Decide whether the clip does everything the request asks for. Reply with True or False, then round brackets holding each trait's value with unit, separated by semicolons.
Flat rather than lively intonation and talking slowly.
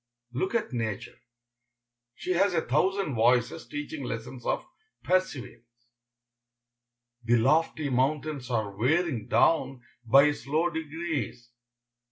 False (5.1 semitones; 105 wpm)